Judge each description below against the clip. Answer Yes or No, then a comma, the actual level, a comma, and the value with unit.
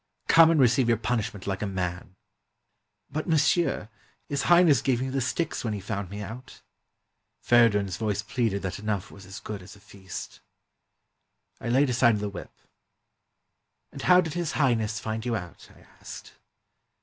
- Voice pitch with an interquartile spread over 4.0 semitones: Yes, average, 5.0 semitones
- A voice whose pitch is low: Yes, low, 110 Hz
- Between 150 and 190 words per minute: Yes, average, 165 wpm